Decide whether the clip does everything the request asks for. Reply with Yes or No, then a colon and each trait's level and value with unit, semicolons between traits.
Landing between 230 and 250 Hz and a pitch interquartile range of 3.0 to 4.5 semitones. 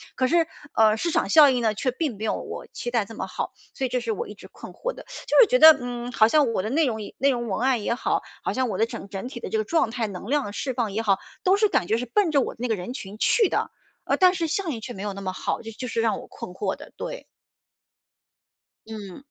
No: high, 240 Hz; average, 5.1 semitones